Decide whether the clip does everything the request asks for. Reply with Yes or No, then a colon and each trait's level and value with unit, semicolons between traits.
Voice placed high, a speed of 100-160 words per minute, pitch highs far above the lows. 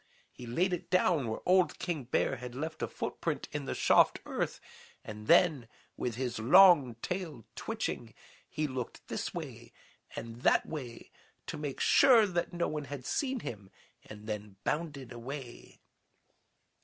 No: medium, 140 Hz; average, 155 wpm; wide, 6.4 semitones